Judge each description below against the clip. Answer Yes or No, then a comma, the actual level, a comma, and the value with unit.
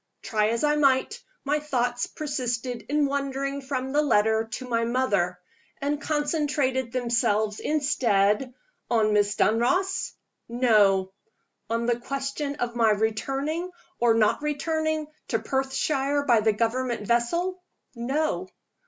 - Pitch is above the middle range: Yes, very high, 255 Hz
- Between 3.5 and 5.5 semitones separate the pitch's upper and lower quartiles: Yes, average, 4.2 semitones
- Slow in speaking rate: Yes, slow, 125 wpm